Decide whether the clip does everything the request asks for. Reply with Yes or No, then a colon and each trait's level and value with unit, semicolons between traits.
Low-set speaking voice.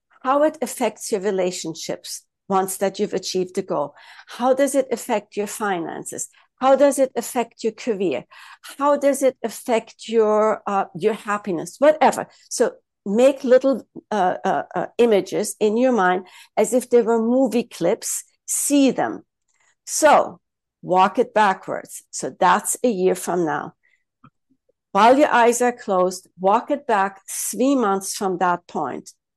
No: high, 230 Hz